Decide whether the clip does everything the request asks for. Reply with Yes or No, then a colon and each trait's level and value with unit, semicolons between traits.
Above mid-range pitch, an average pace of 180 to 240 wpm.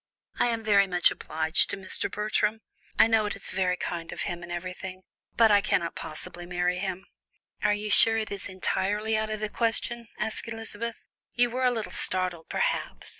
Yes: high, 205 Hz; average, 190 wpm